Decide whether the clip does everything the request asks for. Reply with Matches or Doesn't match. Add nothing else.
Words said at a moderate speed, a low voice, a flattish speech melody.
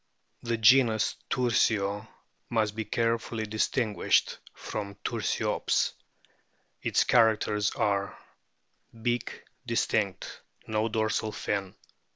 Doesn't match